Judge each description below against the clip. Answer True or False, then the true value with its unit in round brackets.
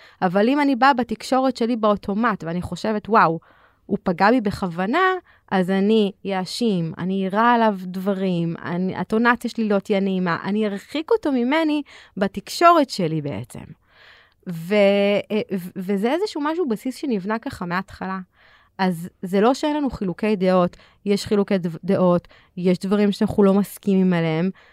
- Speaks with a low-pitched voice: False (200 Hz)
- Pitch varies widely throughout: False (3.7 semitones)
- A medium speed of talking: True (140 wpm)